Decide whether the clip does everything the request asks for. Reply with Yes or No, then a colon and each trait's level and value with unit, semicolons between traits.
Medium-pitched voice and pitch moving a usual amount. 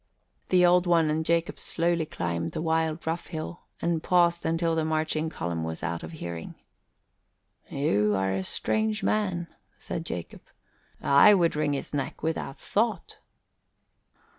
Yes: medium, 160 Hz; average, 3.8 semitones